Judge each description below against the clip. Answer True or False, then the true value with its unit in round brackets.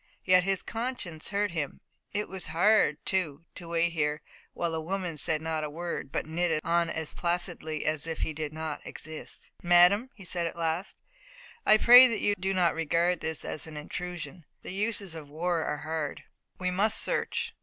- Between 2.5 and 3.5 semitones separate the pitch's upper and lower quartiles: True (2.9 semitones)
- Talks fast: False (185 wpm)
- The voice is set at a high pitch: False (170 Hz)